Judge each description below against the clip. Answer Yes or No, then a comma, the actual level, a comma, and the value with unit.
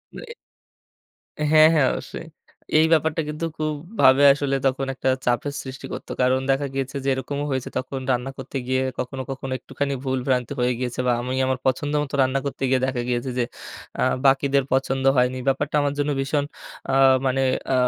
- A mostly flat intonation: Yes, narrow, 1.6 semitones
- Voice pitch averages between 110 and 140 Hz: Yes, low, 135 Hz